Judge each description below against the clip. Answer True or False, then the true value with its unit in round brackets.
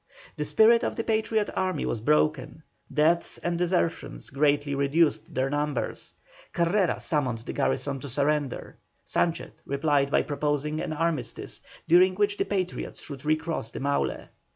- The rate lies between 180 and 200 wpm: False (145 wpm)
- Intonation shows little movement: False (3.5 semitones)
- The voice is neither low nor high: True (150 Hz)